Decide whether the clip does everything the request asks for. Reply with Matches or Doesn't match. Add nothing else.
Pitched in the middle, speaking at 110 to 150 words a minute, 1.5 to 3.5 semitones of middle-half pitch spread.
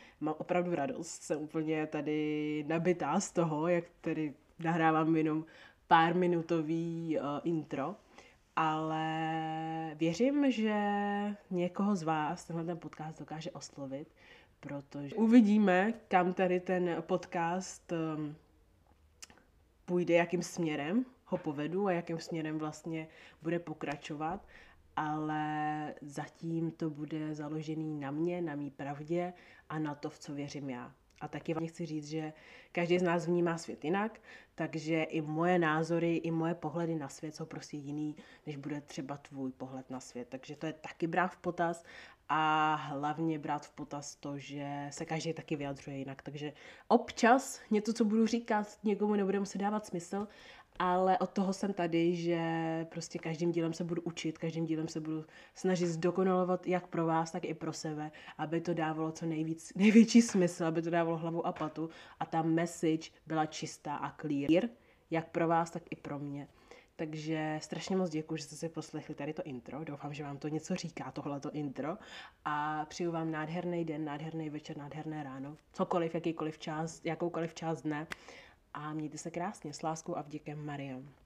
Doesn't match